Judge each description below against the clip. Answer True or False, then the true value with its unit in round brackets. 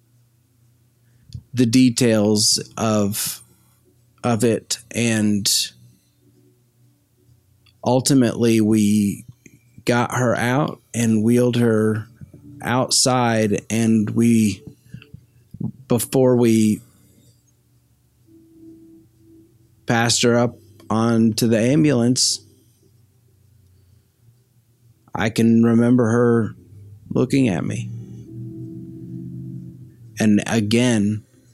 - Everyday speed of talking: False (65 wpm)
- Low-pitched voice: True (115 Hz)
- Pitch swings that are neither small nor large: False (2.2 semitones)